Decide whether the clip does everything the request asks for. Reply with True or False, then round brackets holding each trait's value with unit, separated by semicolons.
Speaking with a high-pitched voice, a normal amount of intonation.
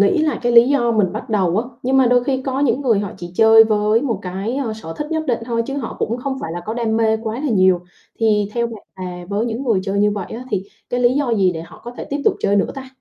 True (225 Hz; 3.6 semitones)